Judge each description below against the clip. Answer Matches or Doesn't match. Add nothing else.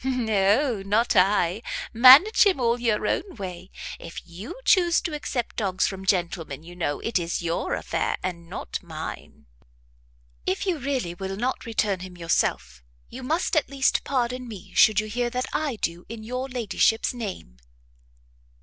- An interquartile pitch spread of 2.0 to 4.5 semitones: Doesn't match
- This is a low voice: Doesn't match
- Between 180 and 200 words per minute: Doesn't match